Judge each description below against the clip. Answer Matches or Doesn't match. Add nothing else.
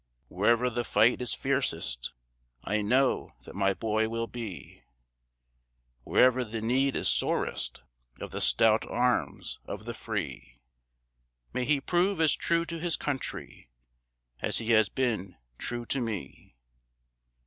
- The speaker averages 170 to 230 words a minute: Doesn't match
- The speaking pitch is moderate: Doesn't match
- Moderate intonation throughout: Matches